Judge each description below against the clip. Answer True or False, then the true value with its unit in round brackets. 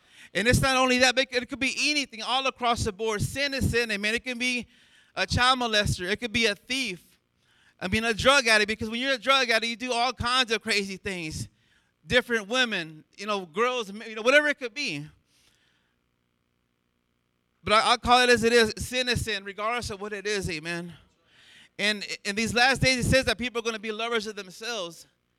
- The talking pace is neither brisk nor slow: False (215 wpm)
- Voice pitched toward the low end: False (225 Hz)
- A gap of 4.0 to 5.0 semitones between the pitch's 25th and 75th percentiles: True (4.6 semitones)